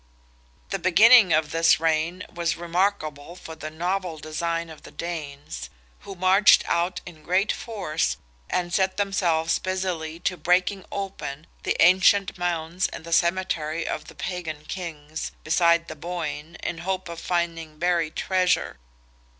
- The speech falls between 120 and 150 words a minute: Yes, average, 140 wpm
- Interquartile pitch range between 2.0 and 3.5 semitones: Yes, narrow, 2.6 semitones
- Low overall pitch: No, medium, 170 Hz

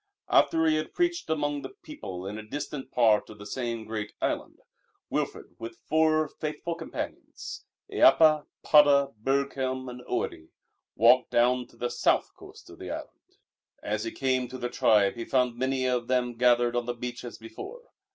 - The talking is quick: No, average, 170 wpm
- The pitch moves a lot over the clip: No, average, 3.9 semitones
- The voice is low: Yes, low, 125 Hz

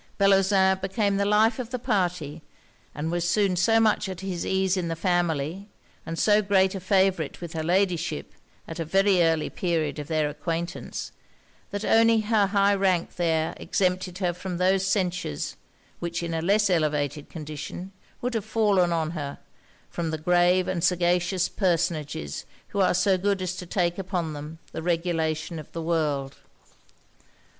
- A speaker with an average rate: Yes, average, 165 wpm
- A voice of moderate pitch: Yes, medium, 180 Hz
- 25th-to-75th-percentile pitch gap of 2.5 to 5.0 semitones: Yes, average, 2.9 semitones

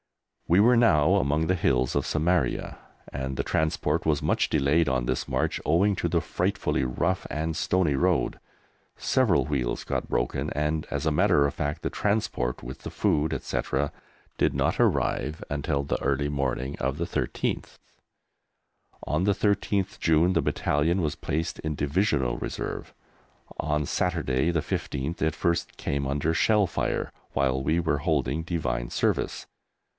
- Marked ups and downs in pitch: No, average, 3.6 semitones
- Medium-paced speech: Yes, average, 155 wpm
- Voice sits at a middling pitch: No, very low, 75 Hz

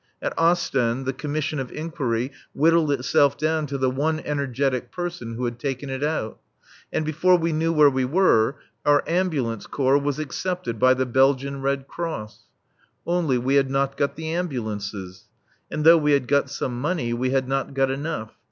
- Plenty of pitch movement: No, average, 3.4 semitones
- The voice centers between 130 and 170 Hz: Yes, medium, 140 Hz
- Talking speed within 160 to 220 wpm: Yes, average, 180 wpm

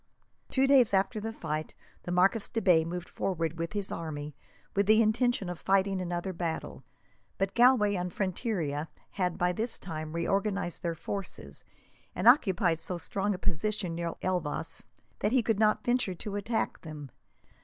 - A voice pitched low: No, high, 190 Hz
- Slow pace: No, average, 165 wpm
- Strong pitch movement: No, average, 4.0 semitones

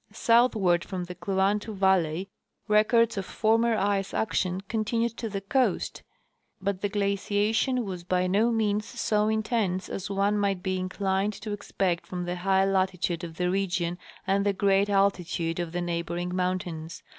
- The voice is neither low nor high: No, high, 195 Hz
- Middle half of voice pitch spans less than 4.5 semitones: Yes, narrow, 2.5 semitones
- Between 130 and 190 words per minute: Yes, average, 155 wpm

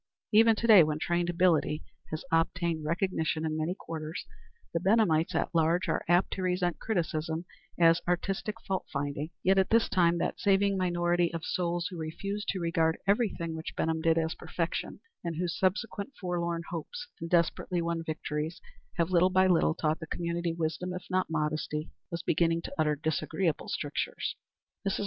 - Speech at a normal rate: Yes, average, 170 wpm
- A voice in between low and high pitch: Yes, medium, 170 Hz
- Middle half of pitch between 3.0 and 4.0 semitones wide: No, narrow, 2.4 semitones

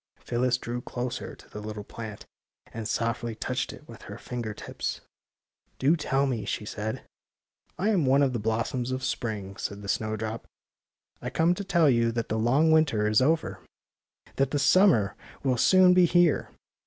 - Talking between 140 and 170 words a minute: No, average, 185 wpm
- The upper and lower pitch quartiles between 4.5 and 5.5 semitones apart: Yes, average, 5.0 semitones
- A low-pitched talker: Yes, low, 120 Hz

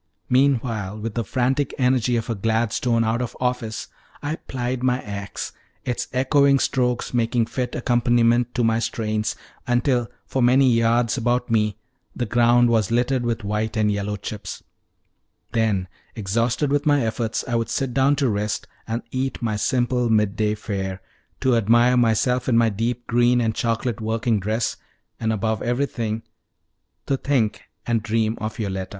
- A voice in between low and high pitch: No, low, 115 Hz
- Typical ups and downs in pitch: No, narrow, 2.2 semitones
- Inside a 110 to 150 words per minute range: No, average, 160 wpm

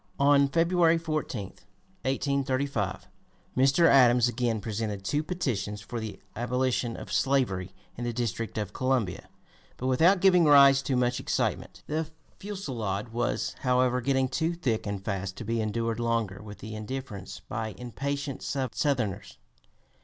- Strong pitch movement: No, average, 4.3 semitones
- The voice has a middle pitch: No, low, 125 Hz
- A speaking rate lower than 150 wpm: Yes, average, 140 wpm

